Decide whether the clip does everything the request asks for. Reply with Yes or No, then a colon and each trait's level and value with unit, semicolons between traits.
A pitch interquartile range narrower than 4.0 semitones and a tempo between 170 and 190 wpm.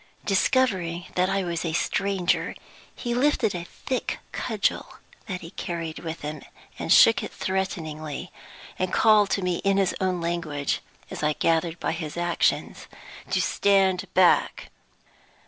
No: average, 2.8 semitones; average, 140 wpm